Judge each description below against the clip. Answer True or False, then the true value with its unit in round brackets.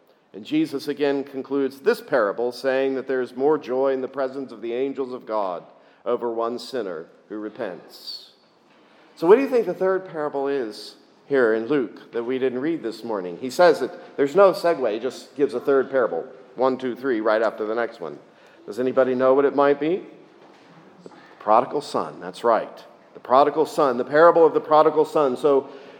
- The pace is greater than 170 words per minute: True (195 wpm)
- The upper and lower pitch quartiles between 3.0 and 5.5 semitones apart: False (2.6 semitones)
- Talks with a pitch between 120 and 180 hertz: True (135 Hz)